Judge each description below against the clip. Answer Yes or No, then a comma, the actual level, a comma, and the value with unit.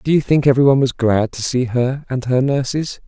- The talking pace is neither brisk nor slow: No, fast, 235 wpm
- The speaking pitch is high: No, low, 130 Hz